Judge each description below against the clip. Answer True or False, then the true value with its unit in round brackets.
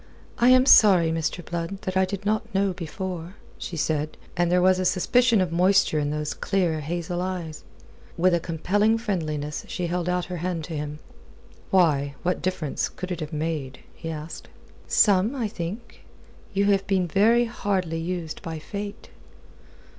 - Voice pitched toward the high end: False (180 Hz)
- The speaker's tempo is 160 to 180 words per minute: True (170 wpm)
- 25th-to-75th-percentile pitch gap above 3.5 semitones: False (3.2 semitones)